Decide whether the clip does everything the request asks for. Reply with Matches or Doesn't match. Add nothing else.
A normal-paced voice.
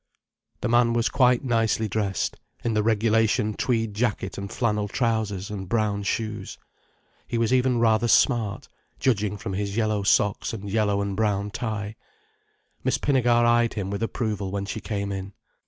Matches